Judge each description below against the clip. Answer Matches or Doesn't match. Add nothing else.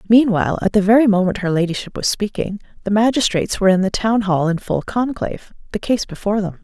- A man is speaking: Doesn't match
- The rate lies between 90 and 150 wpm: Doesn't match